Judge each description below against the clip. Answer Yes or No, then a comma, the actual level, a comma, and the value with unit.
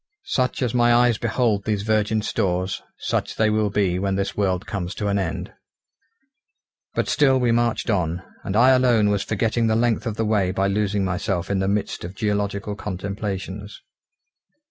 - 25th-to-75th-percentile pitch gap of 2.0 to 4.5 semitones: Yes, narrow, 2.6 semitones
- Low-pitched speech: Yes, low, 105 Hz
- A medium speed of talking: Yes, average, 175 wpm